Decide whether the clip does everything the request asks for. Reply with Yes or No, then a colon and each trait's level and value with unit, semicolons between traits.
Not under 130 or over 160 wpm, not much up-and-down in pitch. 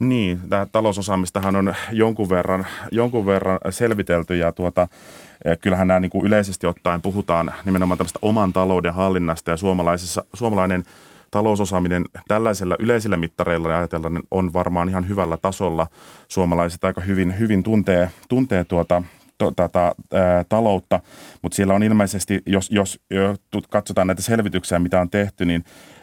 Yes: average, 140 wpm; narrow, 2.3 semitones